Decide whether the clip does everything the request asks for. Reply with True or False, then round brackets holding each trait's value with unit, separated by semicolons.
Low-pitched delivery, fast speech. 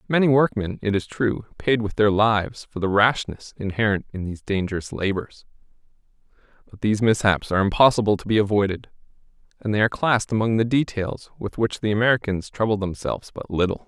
False (105 Hz; 175 wpm)